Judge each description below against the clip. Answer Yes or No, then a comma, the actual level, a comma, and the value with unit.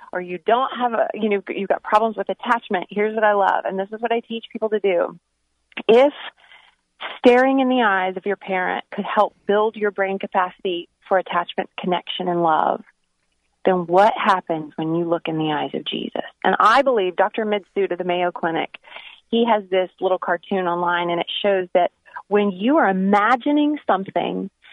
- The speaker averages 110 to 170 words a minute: No, average, 190 wpm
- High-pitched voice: Yes, high, 195 Hz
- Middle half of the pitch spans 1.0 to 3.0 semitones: No, average, 3.9 semitones